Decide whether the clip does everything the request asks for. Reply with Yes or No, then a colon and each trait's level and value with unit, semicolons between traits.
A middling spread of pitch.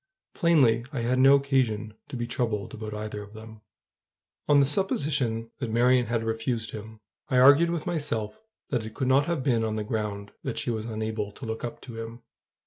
Yes: average, 3.5 semitones